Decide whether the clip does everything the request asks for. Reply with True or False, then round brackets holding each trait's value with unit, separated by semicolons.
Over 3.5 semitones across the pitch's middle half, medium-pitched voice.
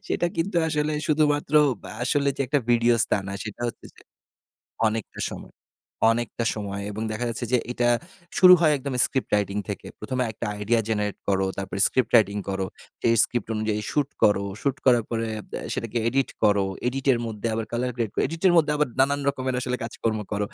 False (4.3 semitones; 120 Hz)